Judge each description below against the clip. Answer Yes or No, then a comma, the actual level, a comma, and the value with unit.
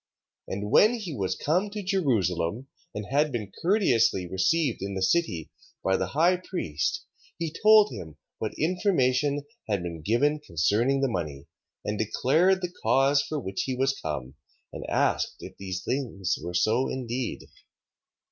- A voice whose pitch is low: Yes, low, 125 Hz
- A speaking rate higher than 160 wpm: No, average, 155 wpm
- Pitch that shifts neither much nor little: No, wide, 8.7 semitones